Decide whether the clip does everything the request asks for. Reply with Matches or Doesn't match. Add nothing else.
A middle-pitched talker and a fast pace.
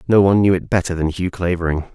Doesn't match